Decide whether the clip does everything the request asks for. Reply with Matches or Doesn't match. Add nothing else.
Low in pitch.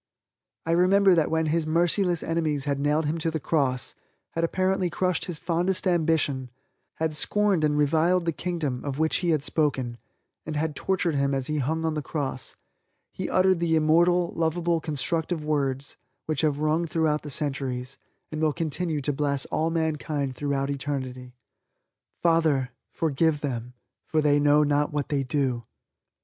Doesn't match